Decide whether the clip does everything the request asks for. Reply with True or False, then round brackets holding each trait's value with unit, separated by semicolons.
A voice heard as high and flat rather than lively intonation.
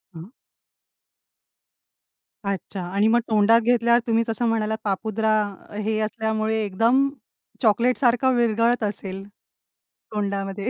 True (220 Hz; 2.3 semitones)